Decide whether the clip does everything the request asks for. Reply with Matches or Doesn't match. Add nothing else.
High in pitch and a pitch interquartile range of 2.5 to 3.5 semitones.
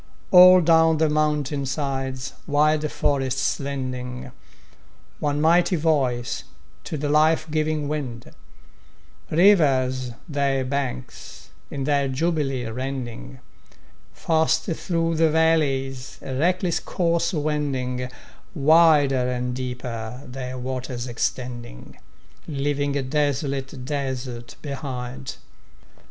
Doesn't match